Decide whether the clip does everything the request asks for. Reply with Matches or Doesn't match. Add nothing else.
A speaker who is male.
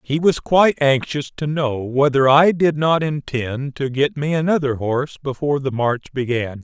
Matches